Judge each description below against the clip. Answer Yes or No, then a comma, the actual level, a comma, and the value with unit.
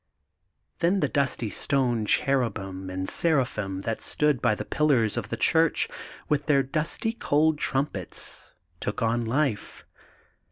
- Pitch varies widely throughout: Yes, wide, 5.9 semitones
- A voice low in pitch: Yes, low, 130 Hz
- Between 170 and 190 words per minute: No, average, 145 wpm